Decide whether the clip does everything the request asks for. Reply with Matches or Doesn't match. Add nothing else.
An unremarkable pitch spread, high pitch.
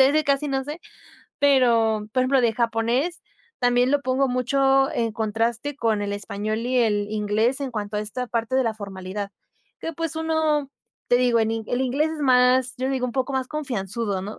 Matches